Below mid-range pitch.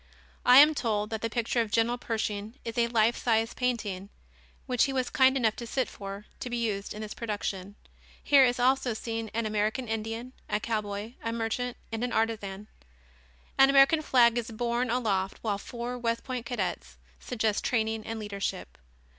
No: high, 230 Hz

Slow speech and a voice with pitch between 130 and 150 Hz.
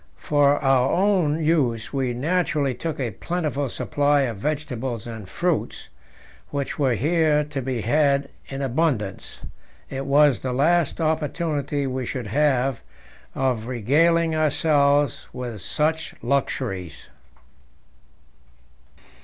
Yes: slow, 110 wpm; medium, 140 Hz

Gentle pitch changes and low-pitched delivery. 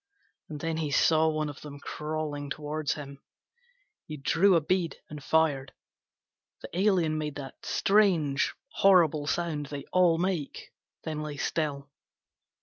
No: narrow, 2.2 semitones; medium, 155 Hz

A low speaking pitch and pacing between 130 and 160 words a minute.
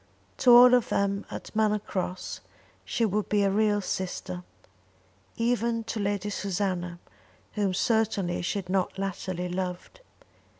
No: high, 200 Hz; slow, 135 wpm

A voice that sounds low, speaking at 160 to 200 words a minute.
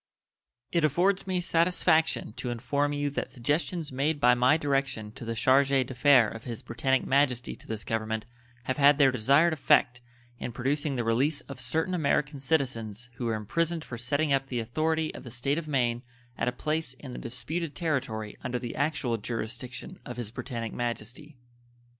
Yes: low, 130 Hz; average, 175 wpm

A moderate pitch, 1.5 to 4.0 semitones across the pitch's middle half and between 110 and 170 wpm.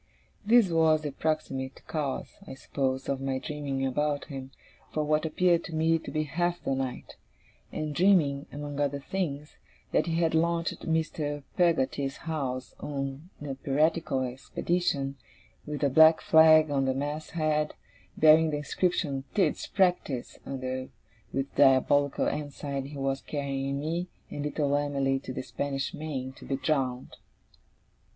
Yes: medium, 145 Hz; average, 2.8 semitones; average, 145 wpm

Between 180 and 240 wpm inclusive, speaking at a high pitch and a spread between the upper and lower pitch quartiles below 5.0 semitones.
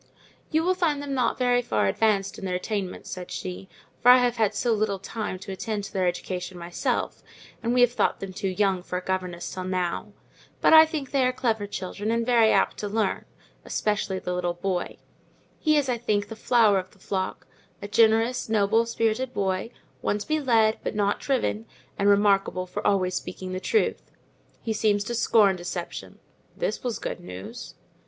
Yes: average, 190 wpm; high, 205 Hz; average, 4.0 semitones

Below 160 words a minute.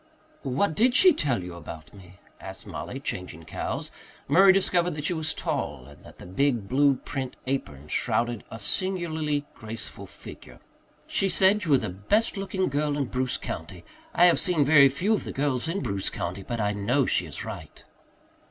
No: average, 185 wpm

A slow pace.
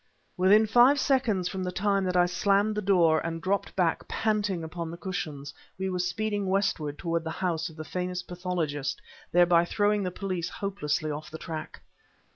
No: average, 180 wpm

